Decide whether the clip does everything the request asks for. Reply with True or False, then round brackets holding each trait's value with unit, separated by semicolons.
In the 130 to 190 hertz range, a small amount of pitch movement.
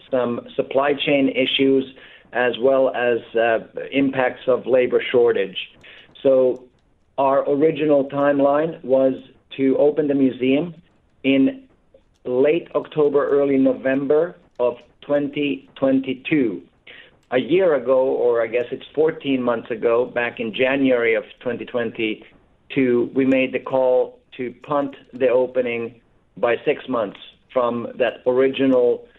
True (135 Hz; 2.2 semitones)